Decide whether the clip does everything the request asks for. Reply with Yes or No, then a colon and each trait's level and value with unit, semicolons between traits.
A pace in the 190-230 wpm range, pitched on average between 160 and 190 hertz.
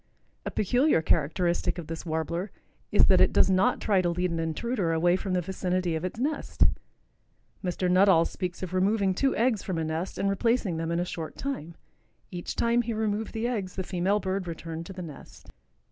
Yes: average, 200 wpm; medium, 185 Hz